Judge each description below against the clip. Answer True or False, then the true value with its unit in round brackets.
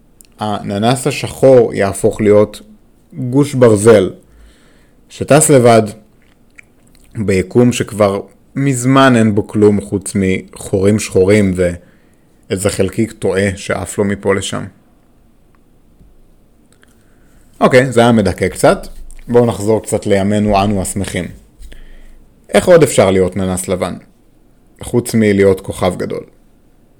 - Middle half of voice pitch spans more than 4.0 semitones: False (3.3 semitones)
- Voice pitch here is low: True (105 Hz)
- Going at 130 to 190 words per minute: False (100 wpm)